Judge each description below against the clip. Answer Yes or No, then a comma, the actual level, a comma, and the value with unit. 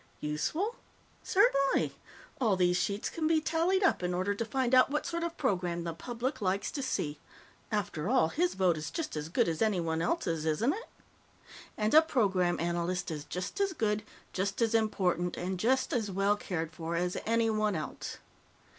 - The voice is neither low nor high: No, high, 200 Hz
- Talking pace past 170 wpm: Yes, average, 180 wpm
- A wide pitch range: Yes, wide, 7.0 semitones